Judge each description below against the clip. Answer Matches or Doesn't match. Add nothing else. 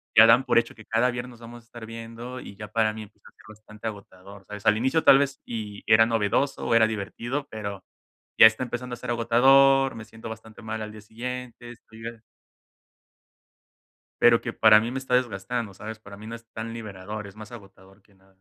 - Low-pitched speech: Matches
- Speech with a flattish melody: Matches